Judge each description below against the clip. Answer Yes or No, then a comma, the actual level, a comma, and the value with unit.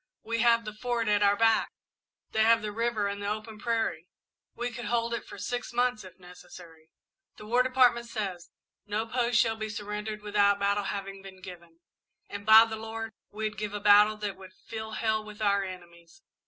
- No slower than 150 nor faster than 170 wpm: No, average, 195 wpm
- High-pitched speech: Yes, high, 215 Hz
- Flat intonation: Yes, narrow, 2.2 semitones